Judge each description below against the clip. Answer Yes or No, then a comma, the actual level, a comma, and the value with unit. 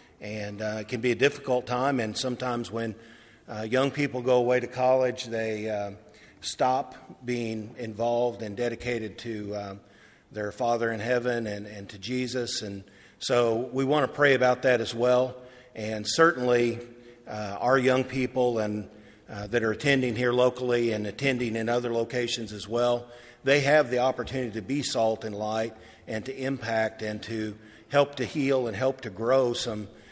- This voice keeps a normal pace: Yes, average, 175 wpm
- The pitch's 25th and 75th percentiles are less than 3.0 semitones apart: Yes, narrow, 2.6 semitones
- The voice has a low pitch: Yes, low, 120 Hz